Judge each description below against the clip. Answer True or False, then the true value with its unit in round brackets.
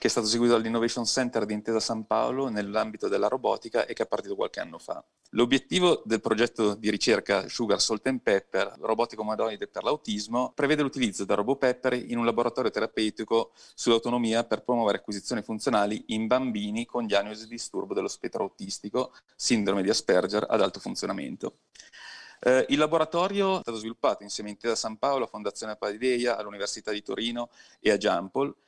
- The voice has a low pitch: True (115 Hz)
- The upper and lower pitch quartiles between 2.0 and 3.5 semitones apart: True (2.8 semitones)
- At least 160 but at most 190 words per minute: True (170 wpm)